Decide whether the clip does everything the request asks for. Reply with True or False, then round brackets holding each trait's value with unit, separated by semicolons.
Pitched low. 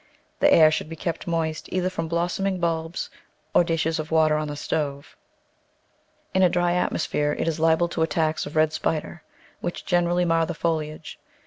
False (165 Hz)